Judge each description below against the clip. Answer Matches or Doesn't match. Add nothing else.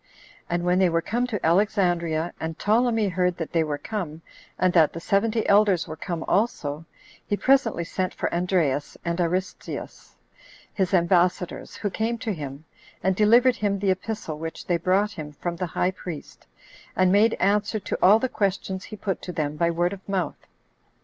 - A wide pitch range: Doesn't match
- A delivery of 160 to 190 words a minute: Matches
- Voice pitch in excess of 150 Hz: Matches